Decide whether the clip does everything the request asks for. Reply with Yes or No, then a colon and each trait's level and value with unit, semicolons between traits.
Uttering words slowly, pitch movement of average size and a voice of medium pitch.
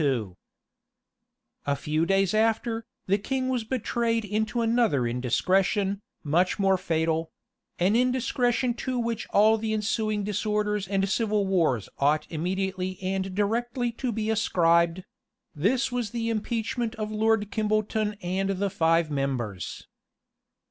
No: slow, 130 wpm; average, 3.8 semitones; high, 210 Hz